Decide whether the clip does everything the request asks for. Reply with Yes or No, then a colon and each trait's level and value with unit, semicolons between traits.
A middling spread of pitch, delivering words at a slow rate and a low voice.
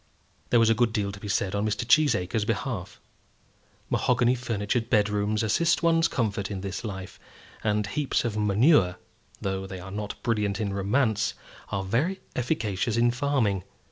No: average, 3.2 semitones; average, 160 wpm; low, 105 Hz